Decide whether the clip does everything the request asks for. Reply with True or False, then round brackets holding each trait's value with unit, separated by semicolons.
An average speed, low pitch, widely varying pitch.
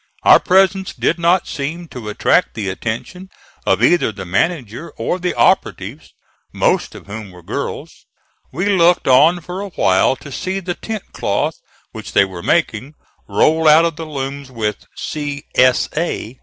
False (165 wpm; 150 Hz; 7.7 semitones)